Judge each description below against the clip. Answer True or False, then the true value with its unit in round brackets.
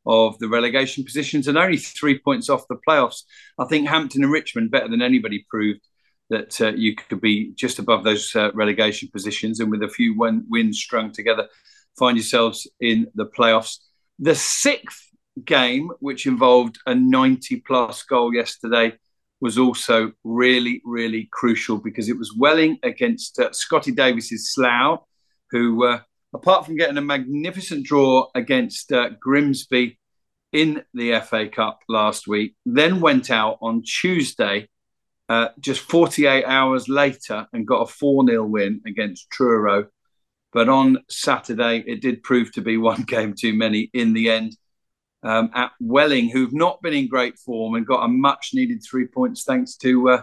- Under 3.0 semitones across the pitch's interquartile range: False (5.2 semitones)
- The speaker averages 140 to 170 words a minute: True (165 wpm)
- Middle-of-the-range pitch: False (125 Hz)